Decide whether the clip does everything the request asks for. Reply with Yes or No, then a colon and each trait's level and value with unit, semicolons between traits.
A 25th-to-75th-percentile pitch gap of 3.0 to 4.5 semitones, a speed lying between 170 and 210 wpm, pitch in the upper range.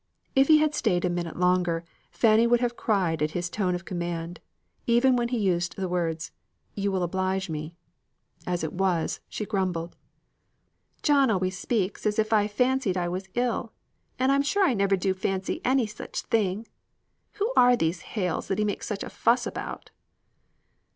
No: average, 4.9 semitones; average, 180 wpm; high, 195 Hz